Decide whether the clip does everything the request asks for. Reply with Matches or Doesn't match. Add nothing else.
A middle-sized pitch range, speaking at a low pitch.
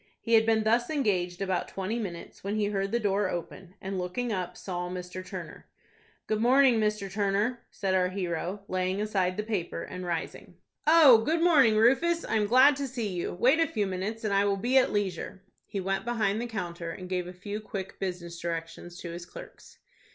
Doesn't match